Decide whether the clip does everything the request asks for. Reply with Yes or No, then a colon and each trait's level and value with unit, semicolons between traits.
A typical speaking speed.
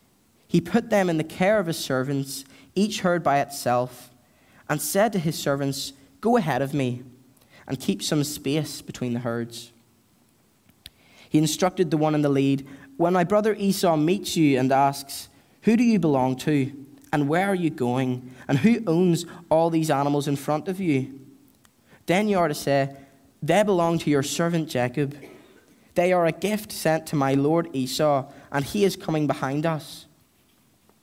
Yes: average, 175 wpm